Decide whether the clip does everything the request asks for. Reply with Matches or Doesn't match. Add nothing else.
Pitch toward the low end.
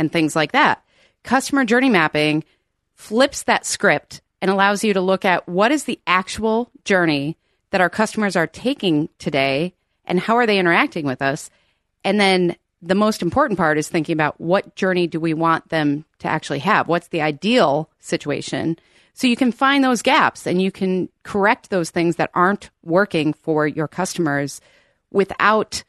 Doesn't match